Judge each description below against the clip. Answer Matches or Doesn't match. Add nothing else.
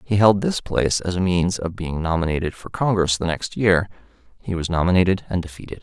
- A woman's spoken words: Doesn't match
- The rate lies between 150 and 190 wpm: Doesn't match